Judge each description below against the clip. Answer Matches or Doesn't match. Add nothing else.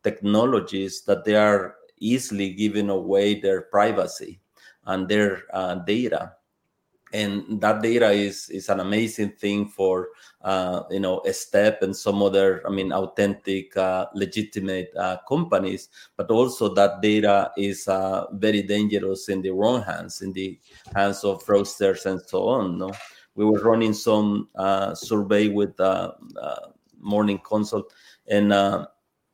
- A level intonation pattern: Matches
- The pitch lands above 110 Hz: Doesn't match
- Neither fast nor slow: Matches